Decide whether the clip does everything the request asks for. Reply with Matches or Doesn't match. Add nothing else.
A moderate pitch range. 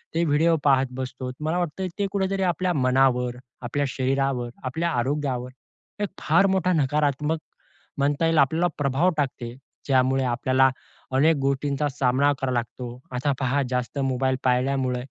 Matches